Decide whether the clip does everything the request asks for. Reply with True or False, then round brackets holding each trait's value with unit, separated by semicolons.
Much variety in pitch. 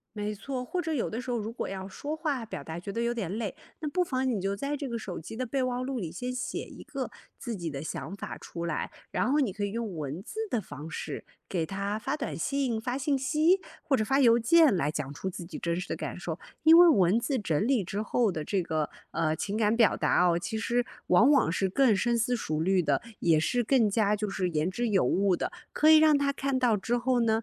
True (5.8 semitones)